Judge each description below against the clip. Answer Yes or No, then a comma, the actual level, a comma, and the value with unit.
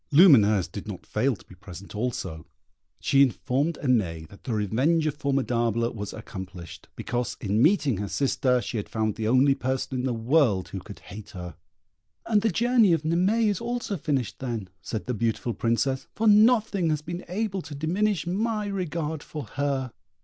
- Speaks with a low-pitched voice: Yes, low, 130 Hz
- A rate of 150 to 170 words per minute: No, average, 180 wpm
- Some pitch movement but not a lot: No, wide, 7.8 semitones